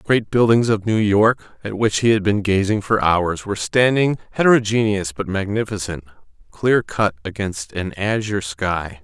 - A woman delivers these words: No, male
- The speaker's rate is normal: Yes, average, 165 wpm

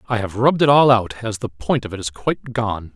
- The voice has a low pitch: Yes, low, 115 Hz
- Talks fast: Yes, fast, 285 wpm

